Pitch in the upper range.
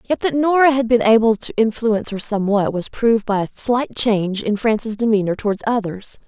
Yes: high, 220 Hz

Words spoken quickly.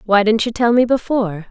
Yes: fast, 240 wpm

